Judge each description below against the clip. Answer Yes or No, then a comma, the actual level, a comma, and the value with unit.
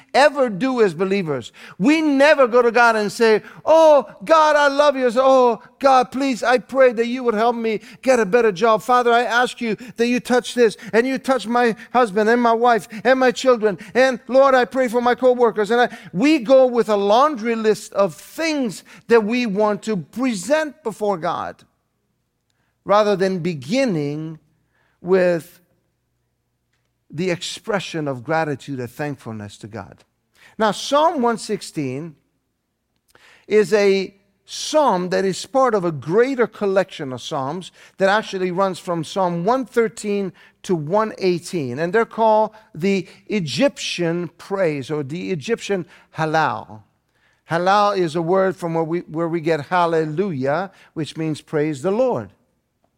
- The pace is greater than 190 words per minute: No, average, 155 wpm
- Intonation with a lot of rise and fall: Yes, wide, 6.1 semitones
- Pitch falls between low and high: No, high, 210 Hz